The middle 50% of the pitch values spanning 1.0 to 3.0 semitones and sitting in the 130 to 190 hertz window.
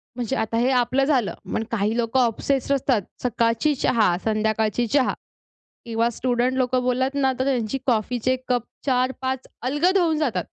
No: narrow, 2.4 semitones; very high, 250 Hz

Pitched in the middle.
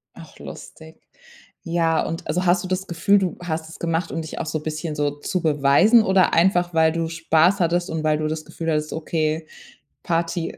Yes: medium, 165 Hz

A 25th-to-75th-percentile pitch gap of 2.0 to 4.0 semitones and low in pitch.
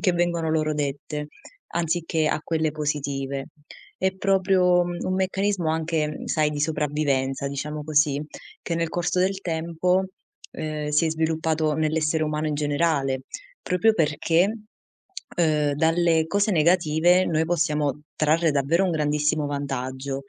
No: narrow, 2.5 semitones; medium, 155 Hz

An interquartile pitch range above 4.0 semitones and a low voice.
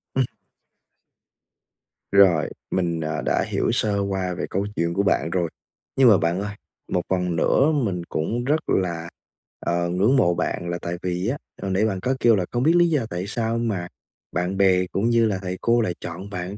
Yes: average, 4.4 semitones; very low, 95 Hz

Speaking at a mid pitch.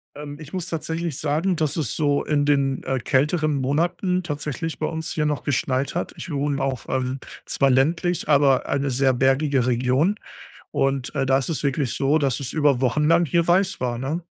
Yes: medium, 145 Hz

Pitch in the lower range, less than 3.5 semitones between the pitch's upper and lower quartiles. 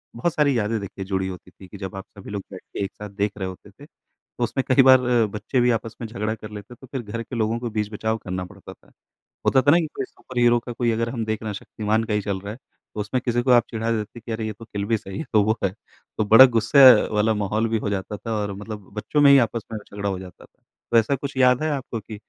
Yes: low, 110 Hz; average, 2.8 semitones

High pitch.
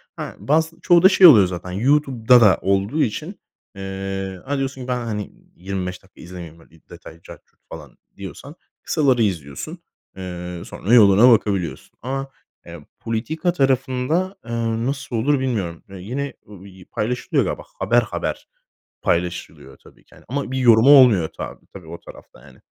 No: low, 110 Hz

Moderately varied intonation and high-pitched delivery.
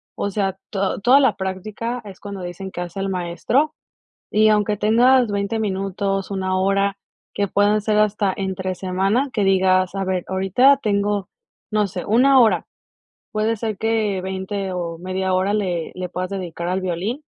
No: narrow, 2.2 semitones; high, 195 Hz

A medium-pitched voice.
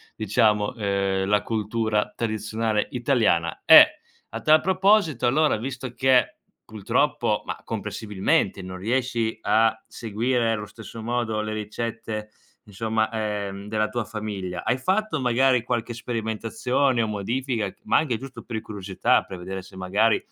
No: low, 110 Hz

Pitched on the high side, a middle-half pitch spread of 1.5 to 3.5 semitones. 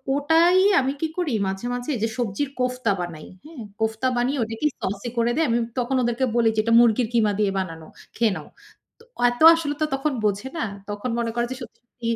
No: high, 240 Hz; average, 3.9 semitones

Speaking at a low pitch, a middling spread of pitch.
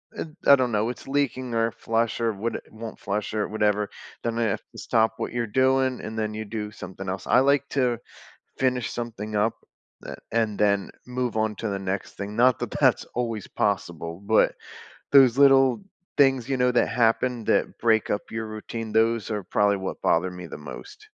Yes: low, 115 Hz; average, 3.0 semitones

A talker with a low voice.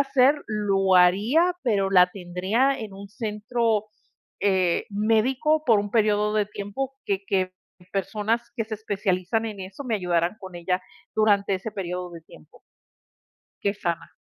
No: high, 205 Hz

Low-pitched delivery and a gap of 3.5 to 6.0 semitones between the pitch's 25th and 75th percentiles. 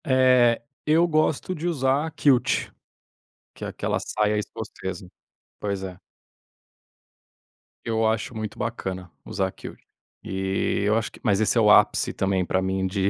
Yes: low, 105 Hz; average, 5.2 semitones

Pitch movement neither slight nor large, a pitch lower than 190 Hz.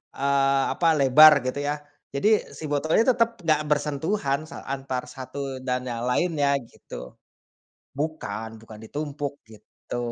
Yes: average, 3.2 semitones; medium, 140 Hz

